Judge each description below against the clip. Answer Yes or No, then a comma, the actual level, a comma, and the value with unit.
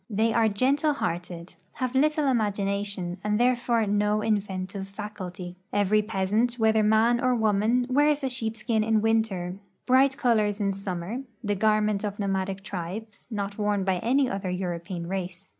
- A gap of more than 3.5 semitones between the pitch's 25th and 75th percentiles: No, average, 2.9 semitones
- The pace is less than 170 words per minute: Yes, average, 150 wpm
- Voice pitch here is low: No, high, 210 Hz